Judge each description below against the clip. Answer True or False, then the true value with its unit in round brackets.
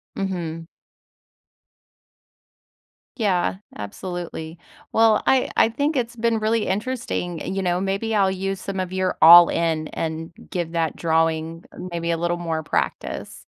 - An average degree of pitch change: True (3.7 semitones)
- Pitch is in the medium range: True (180 Hz)